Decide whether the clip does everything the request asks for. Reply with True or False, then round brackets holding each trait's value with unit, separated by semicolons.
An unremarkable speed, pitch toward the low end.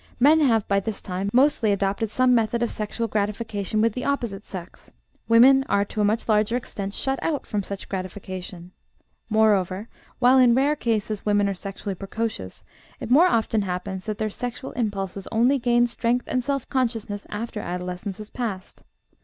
False (170 wpm; 215 Hz)